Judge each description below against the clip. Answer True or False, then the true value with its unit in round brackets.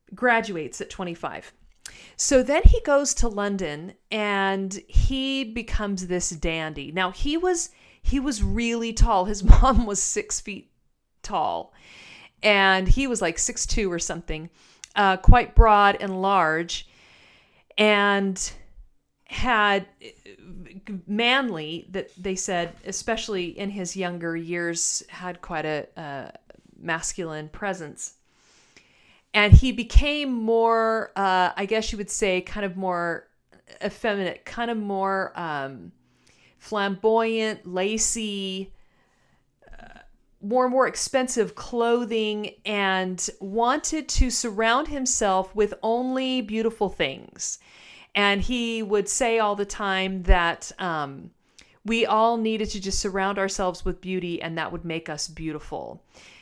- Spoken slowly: True (125 wpm)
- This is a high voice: True (200 Hz)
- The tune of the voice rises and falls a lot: False (3.7 semitones)